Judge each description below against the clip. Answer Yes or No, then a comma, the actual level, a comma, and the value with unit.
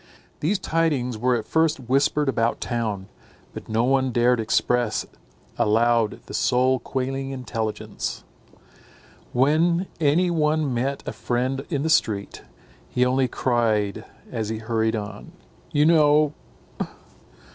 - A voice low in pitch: Yes, low, 125 Hz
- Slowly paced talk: Yes, slow, 125 wpm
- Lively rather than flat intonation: No, average, 4.5 semitones